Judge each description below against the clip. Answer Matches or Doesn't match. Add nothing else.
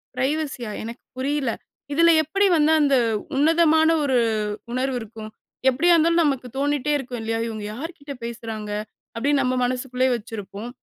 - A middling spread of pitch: Matches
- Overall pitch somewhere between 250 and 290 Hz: Matches